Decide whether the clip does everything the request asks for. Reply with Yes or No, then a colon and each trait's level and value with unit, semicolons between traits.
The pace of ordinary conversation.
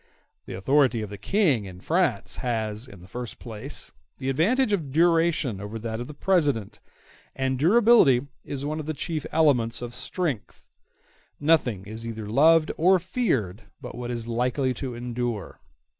Yes: average, 160 wpm